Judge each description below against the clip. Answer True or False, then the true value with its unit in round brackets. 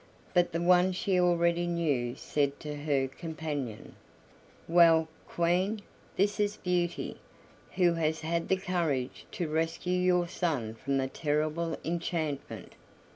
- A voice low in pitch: False (170 Hz)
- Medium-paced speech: False (130 wpm)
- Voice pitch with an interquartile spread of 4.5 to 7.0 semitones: False (2.9 semitones)